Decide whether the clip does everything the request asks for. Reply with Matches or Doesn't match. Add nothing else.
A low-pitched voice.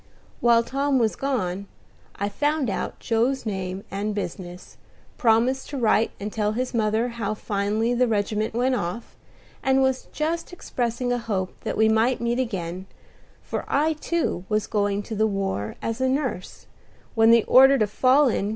Doesn't match